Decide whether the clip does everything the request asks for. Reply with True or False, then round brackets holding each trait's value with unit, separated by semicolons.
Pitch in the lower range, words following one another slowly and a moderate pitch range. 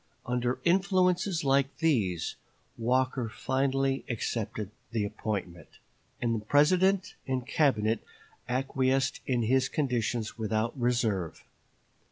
True (125 Hz; 100 wpm; 3.6 semitones)